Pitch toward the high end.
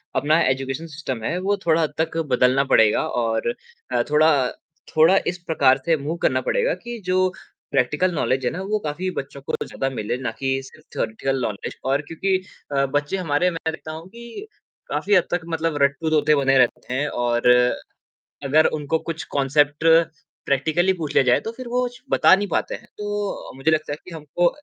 No: medium, 155 Hz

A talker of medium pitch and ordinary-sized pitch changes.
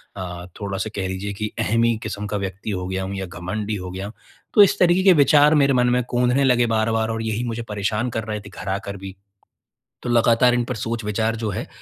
No: low, 110 Hz; average, 3.6 semitones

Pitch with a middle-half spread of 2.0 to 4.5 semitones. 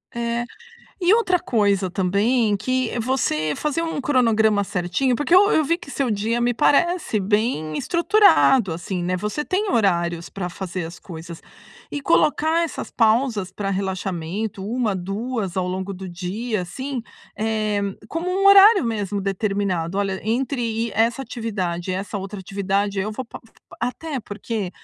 No: average, 5.2 semitones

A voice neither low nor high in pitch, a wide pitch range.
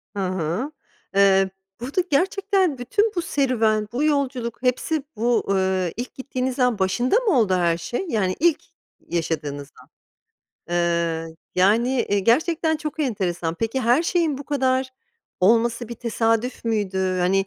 No: high, 235 Hz; wide, 6.3 semitones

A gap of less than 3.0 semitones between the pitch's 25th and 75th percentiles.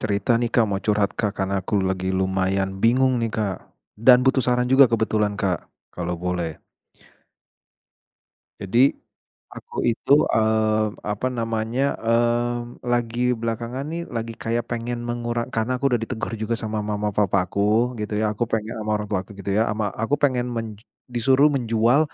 Yes: narrow, 2.6 semitones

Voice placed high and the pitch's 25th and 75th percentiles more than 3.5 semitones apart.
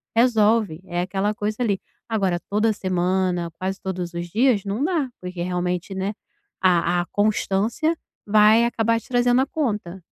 Yes: high, 200 Hz; average, 3.9 semitones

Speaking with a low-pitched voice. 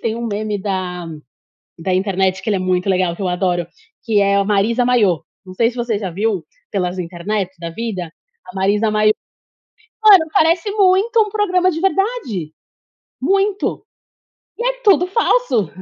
No: high, 210 Hz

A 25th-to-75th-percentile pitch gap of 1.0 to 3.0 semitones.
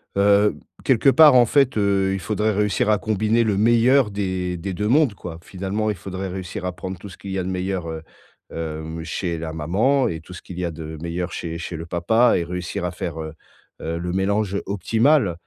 No: average, 3.7 semitones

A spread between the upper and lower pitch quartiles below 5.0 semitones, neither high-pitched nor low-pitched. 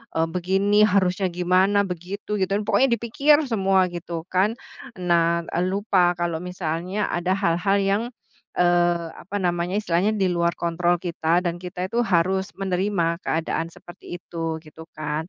Yes: narrow, 2.4 semitones; medium, 180 Hz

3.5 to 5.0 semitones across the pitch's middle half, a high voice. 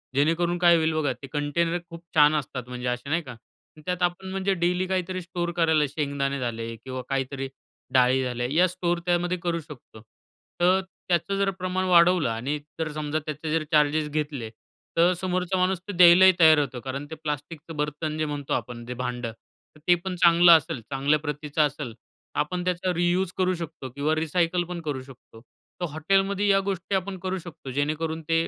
No: average, 3.8 semitones; medium, 160 Hz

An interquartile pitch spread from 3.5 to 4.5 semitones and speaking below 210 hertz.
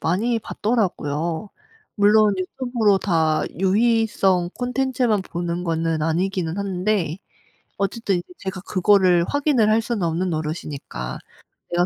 Yes: average, 4.2 semitones; high, 190 Hz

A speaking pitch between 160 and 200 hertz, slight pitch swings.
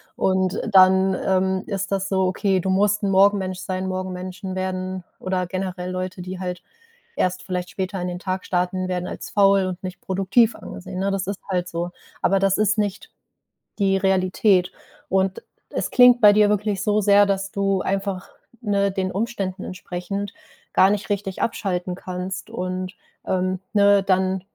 Yes: high, 190 Hz; narrow, 1.3 semitones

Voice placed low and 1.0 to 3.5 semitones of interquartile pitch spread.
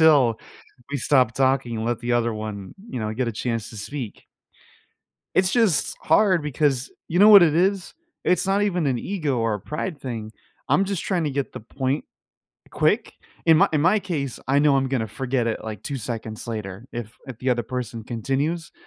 No: low, 130 Hz; wide, 5.6 semitones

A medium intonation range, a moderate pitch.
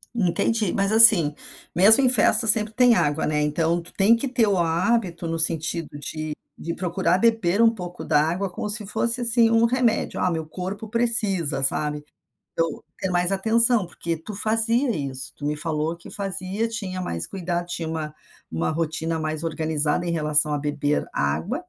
No: wide, 5.8 semitones; medium, 175 Hz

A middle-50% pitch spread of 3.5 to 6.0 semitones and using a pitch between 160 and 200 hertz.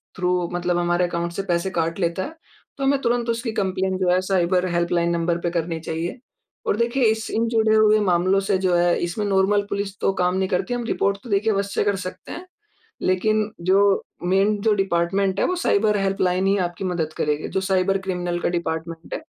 No: average, 2.8 semitones; high, 190 Hz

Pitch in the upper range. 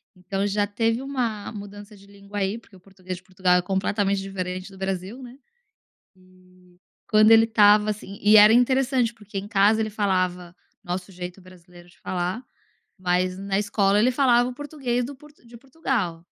Yes: high, 200 Hz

